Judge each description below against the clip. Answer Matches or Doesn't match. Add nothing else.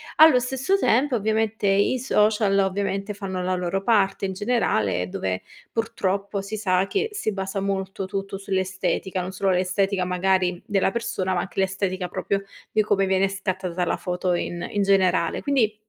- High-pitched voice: Matches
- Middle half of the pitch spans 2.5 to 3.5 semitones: Doesn't match